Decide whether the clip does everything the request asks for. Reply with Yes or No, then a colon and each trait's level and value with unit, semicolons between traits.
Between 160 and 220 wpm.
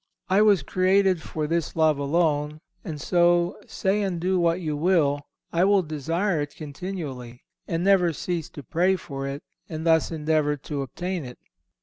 Yes: average, 165 wpm